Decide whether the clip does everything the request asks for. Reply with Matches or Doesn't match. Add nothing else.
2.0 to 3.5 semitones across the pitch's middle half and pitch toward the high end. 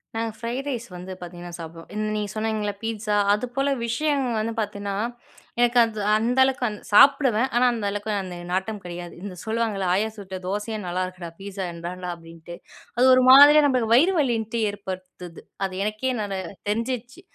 Doesn't match